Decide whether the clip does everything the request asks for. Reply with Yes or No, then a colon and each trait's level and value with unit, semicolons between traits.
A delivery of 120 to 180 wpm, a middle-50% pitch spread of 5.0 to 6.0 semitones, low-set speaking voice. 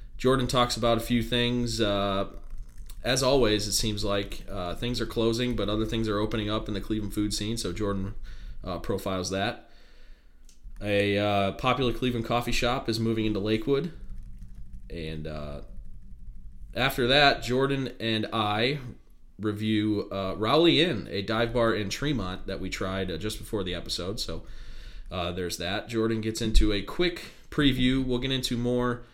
No: average, 165 wpm; average, 3.3 semitones; low, 110 Hz